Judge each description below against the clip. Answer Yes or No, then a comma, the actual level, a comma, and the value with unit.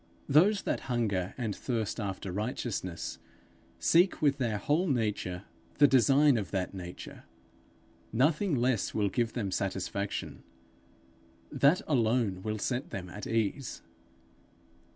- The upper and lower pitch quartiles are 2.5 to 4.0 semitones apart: No, wide, 5.6 semitones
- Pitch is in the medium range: No, low, 115 Hz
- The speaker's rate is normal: No, slow, 120 wpm